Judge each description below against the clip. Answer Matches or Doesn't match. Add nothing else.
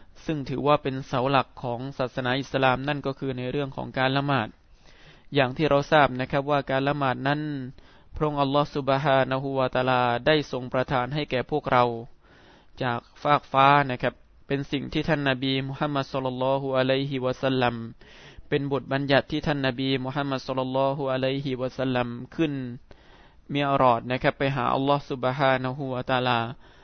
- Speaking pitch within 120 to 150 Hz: Matches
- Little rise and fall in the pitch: Matches